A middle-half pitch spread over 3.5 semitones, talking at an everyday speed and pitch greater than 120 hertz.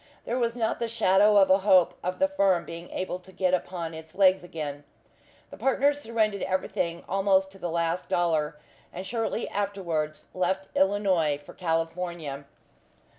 No: average, 3.1 semitones; average, 160 wpm; medium, 185 Hz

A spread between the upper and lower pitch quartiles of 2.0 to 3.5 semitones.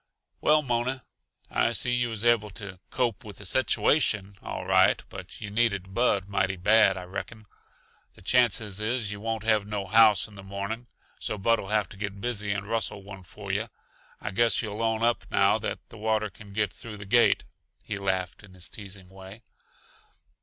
Yes: average, 2.7 semitones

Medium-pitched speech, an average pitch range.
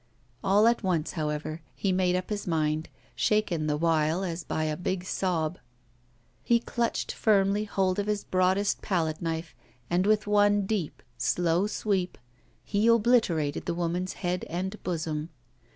Yes: medium, 180 Hz; average, 3.9 semitones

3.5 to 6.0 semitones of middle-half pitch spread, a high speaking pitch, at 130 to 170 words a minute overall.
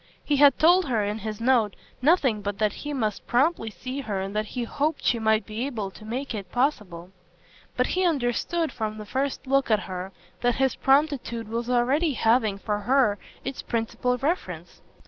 No: average, 4.3 semitones; high, 240 Hz; average, 185 wpm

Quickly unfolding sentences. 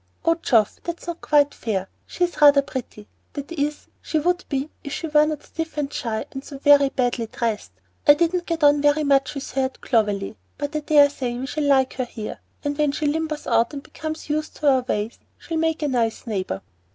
Yes: fast, 215 wpm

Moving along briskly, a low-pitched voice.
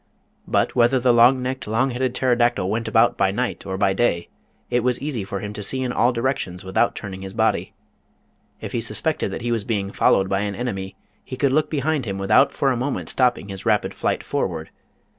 Yes: fast, 230 wpm; low, 120 Hz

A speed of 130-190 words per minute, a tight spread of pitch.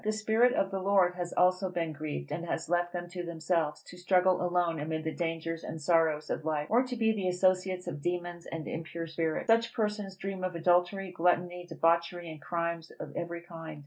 No: fast, 205 wpm; narrow, 2.1 semitones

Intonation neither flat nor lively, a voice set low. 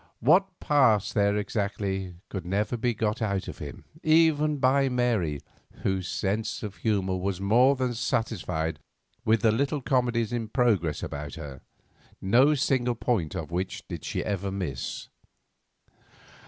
Yes: average, 4.6 semitones; low, 110 Hz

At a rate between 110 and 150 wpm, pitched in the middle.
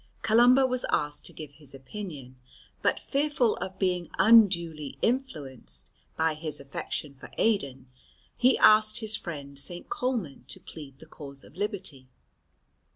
Yes: average, 140 wpm; medium, 170 Hz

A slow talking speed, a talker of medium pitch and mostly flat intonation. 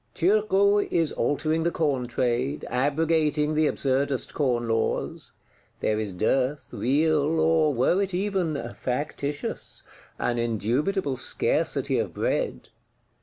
No: slow, 115 wpm; medium, 145 Hz; average, 4.3 semitones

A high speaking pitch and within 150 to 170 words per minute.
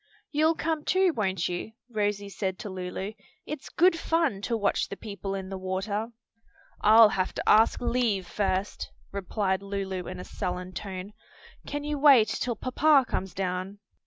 Yes: high, 200 Hz; average, 160 wpm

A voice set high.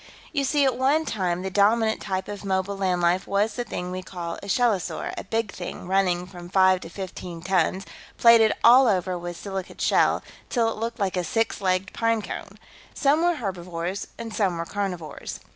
Yes: high, 195 Hz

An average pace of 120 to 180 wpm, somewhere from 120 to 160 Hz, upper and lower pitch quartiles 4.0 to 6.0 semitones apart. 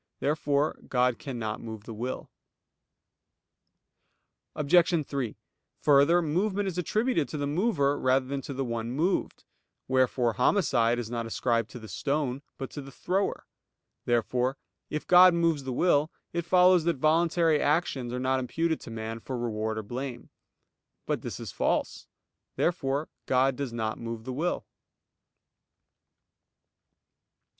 Yes: average, 140 wpm; low, 135 Hz; average, 5.2 semitones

